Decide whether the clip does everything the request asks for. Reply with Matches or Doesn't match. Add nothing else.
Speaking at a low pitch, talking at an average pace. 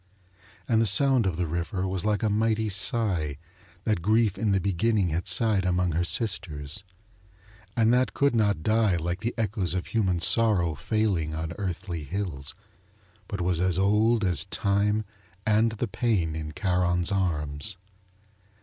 Matches